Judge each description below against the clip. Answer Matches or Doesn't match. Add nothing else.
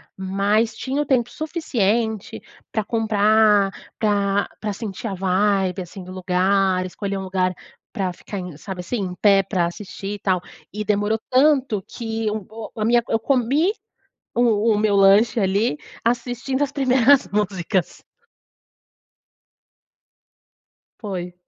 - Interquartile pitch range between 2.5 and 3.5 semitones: Matches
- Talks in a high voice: Matches